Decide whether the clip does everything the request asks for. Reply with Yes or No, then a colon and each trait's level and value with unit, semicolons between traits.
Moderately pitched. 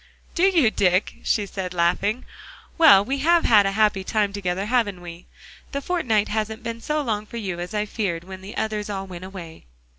No: high, 210 Hz